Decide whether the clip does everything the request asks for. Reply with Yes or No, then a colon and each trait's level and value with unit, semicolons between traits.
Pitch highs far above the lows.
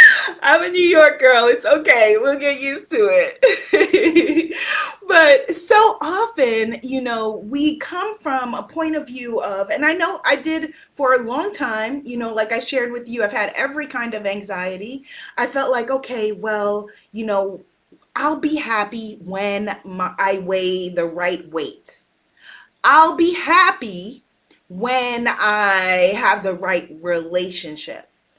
Yes: wide, 7.6 semitones